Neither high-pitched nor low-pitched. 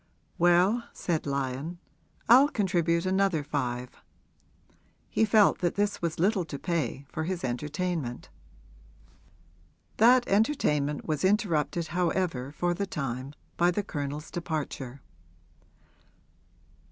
Yes: medium, 170 Hz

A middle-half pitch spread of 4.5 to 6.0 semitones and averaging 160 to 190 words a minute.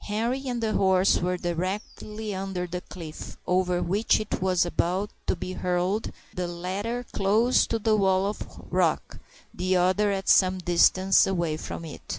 No: average, 2.7 semitones; average, 165 wpm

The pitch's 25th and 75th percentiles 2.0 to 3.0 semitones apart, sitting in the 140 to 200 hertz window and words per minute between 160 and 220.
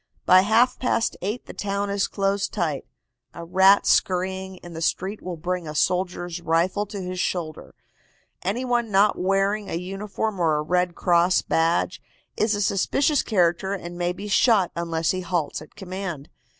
Yes: narrow, 2.6 semitones; medium, 185 Hz; average, 170 wpm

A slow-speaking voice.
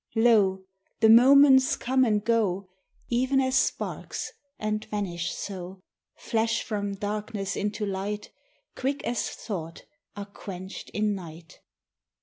Yes: slow, 120 wpm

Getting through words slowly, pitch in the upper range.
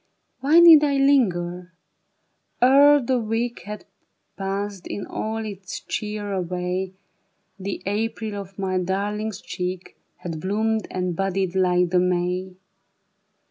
Yes: slow, 120 wpm; high, 195 Hz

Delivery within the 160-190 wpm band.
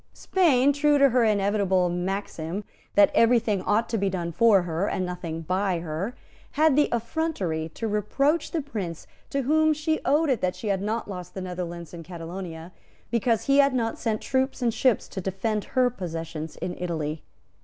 Yes: average, 185 wpm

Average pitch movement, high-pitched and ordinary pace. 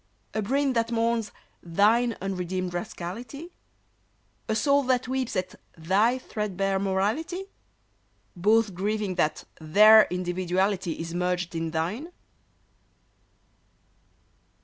No: average, 4.4 semitones; high, 200 Hz; slow, 100 wpm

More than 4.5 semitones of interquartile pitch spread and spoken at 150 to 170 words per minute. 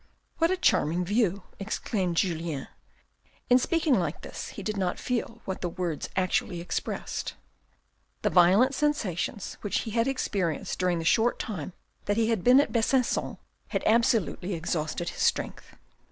Yes: average, 5.1 semitones; average, 155 wpm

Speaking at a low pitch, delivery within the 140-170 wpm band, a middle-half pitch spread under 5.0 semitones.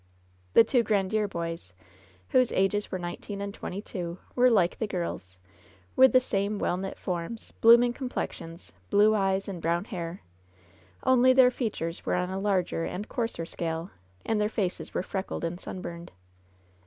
No: high, 195 Hz; average, 165 wpm; average, 4.3 semitones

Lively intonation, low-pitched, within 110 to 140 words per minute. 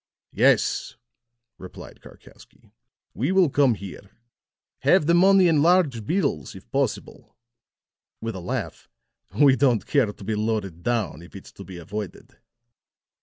Yes: wide, 7.1 semitones; low, 115 Hz; slow, 135 wpm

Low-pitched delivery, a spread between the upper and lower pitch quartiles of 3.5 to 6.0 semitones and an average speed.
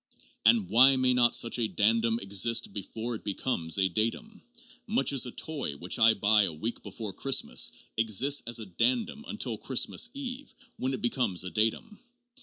Yes: low, 115 Hz; average, 4.0 semitones; average, 175 wpm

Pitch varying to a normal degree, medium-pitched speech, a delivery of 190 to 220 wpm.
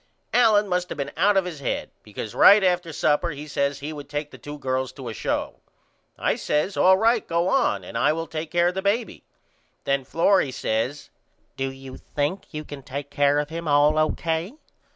Yes: average, 4.2 semitones; medium, 155 Hz; fast, 205 wpm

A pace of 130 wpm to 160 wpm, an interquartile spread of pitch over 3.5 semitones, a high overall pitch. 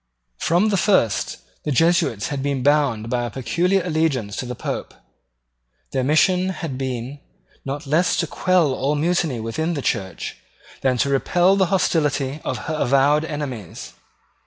No: average, 155 wpm; average, 4.7 semitones; medium, 145 Hz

